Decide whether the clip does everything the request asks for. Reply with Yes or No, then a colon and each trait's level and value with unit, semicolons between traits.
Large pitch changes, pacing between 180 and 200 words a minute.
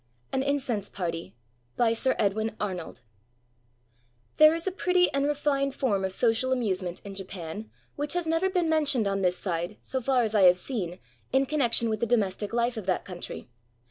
Yes: wide, 6.3 semitones; average, 185 wpm